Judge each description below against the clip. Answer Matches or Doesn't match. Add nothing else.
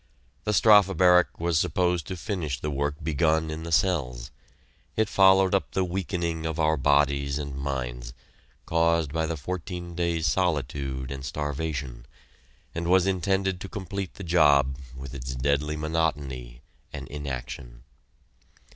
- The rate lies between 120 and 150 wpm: Matches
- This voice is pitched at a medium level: Doesn't match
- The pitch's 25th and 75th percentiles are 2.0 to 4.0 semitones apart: Doesn't match